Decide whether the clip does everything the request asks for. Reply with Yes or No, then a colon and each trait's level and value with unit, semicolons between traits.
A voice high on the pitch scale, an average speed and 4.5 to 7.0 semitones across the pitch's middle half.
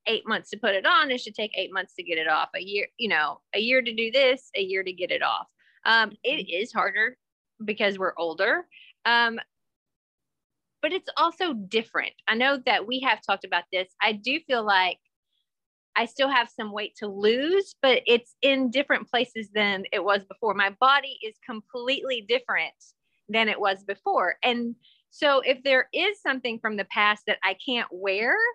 Yes: high, 225 Hz; average, 195 wpm; average, 4.9 semitones